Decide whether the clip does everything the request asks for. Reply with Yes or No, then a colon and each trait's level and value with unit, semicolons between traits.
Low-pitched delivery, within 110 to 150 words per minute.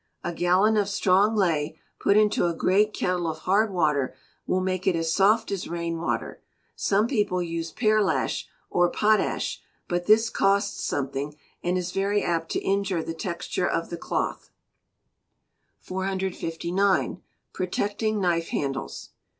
No: medium, 185 Hz; average, 140 wpm